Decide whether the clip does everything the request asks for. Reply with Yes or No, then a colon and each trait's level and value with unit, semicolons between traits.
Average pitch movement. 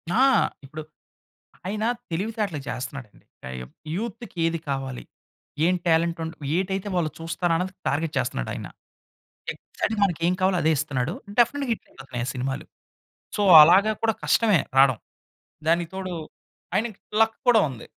No: wide, 6.4 semitones